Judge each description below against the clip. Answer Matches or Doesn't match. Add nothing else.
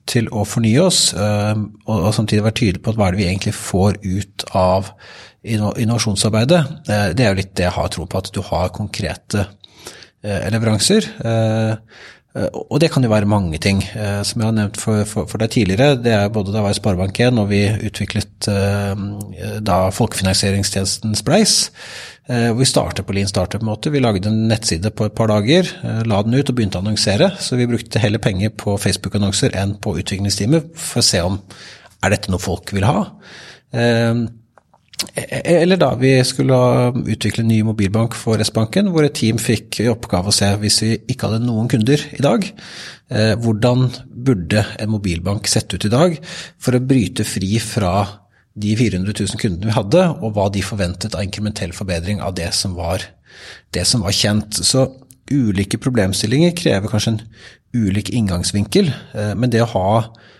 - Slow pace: Doesn't match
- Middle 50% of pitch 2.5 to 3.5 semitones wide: Matches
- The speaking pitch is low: Matches